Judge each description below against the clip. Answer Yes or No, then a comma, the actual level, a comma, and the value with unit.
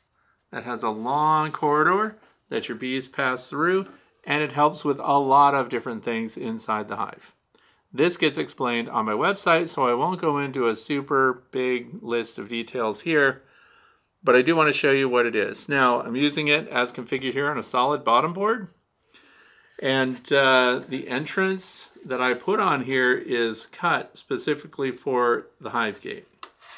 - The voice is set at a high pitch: No, low, 135 Hz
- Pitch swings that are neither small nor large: Yes, average, 3.3 semitones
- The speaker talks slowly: No, average, 175 wpm